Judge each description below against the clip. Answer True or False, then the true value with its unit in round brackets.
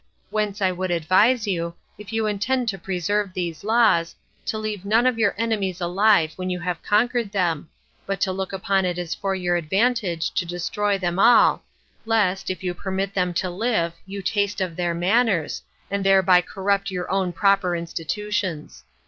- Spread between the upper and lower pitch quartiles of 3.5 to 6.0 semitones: False (2.7 semitones)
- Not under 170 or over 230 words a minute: True (175 wpm)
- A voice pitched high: True (195 Hz)